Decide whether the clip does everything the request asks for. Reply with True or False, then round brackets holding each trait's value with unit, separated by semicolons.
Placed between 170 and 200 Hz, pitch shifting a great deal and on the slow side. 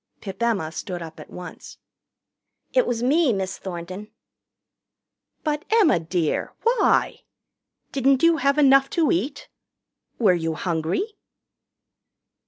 False (225 Hz; 8.4 semitones; 115 wpm)